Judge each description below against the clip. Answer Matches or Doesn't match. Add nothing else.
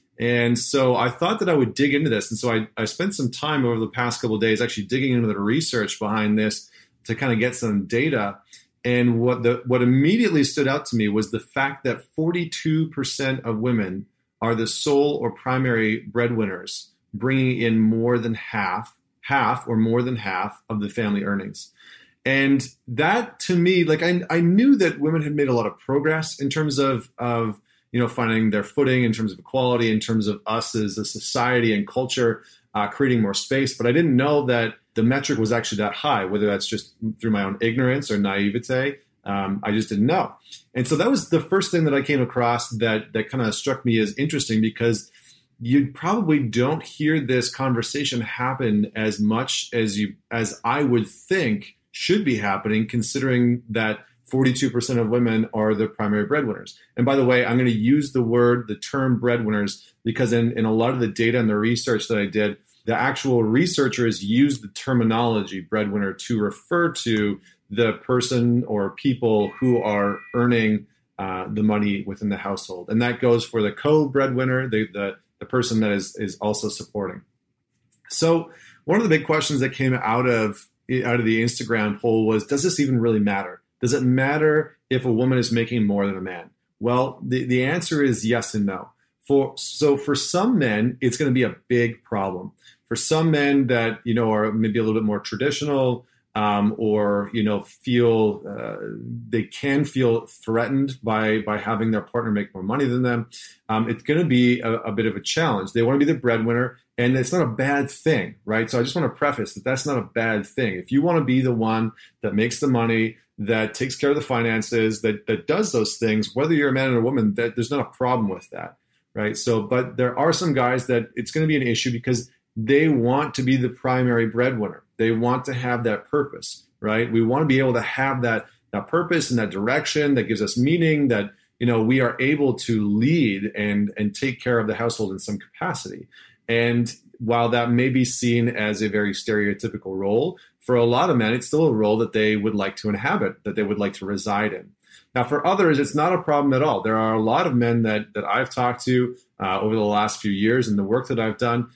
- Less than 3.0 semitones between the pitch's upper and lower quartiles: Doesn't match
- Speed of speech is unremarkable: Doesn't match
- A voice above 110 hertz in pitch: Matches